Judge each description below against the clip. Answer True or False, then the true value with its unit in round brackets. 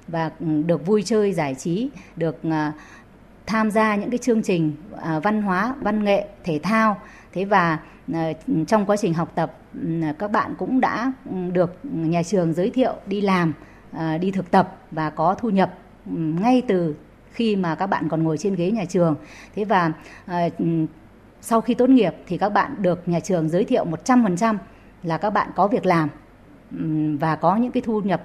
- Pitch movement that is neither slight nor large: True (4.8 semitones)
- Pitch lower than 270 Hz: True (185 Hz)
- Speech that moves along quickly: False (175 wpm)